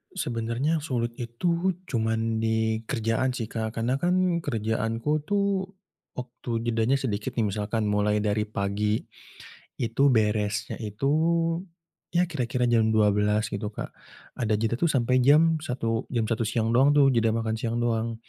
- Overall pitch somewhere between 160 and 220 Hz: No, low, 115 Hz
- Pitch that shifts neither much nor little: Yes, average, 3.0 semitones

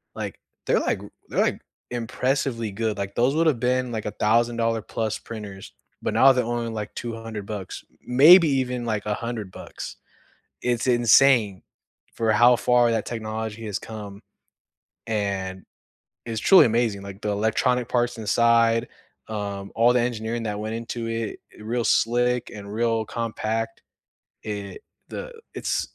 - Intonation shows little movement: Yes, narrow, 2.2 semitones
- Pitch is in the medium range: No, low, 115 Hz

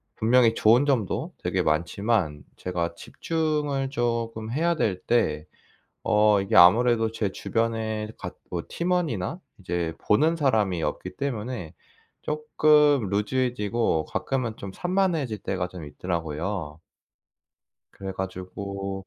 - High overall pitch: No, low, 110 Hz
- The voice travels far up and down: Yes, wide, 6.2 semitones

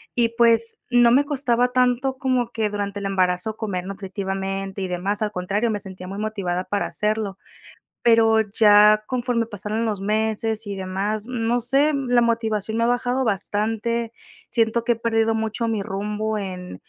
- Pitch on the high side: Yes, high, 220 Hz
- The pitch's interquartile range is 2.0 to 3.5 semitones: Yes, average, 2.8 semitones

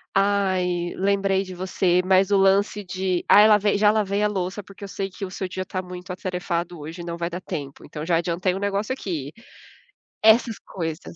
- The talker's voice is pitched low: No, medium, 185 Hz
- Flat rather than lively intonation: Yes, narrow, 2.1 semitones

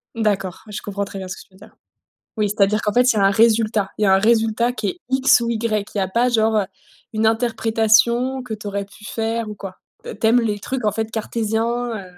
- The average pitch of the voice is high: Yes, high, 220 Hz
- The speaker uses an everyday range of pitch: No, narrow, 2.2 semitones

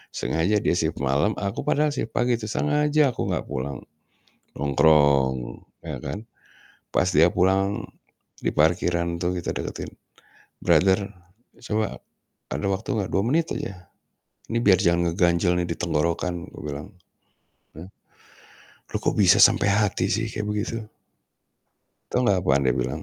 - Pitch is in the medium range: No, very low, 90 Hz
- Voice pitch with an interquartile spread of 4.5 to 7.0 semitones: Yes, average, 4.8 semitones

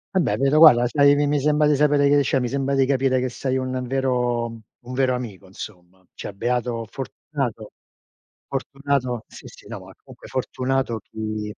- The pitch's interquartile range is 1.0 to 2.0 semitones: No, average, 2.7 semitones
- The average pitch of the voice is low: Yes, low, 130 Hz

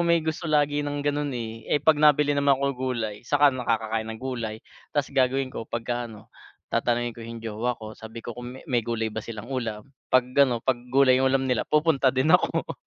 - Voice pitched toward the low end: Yes, low, 125 Hz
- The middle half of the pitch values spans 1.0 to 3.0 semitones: No, average, 3.7 semitones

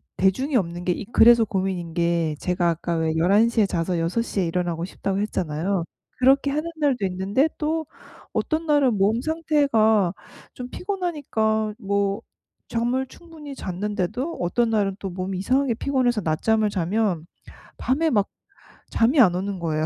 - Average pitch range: No, wide, 6.2 semitones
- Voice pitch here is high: Yes, high, 210 Hz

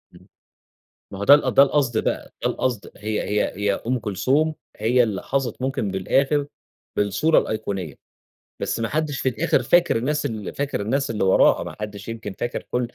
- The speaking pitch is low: Yes, low, 120 Hz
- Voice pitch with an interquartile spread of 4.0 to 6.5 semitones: Yes, average, 4.9 semitones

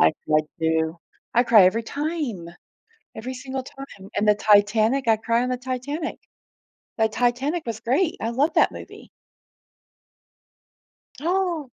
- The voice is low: No, high, 240 Hz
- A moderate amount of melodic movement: Yes, average, 4.4 semitones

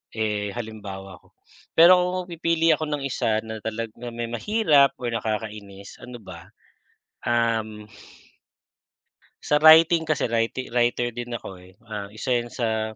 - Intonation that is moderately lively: Yes, average, 4.2 semitones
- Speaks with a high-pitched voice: No, low, 115 Hz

